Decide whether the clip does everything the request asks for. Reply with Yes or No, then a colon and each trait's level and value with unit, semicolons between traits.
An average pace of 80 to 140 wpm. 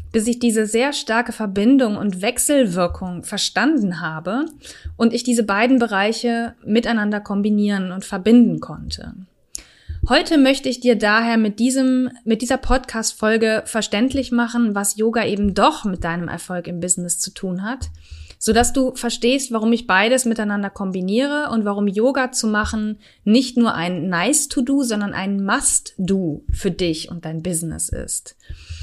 No: average, 155 wpm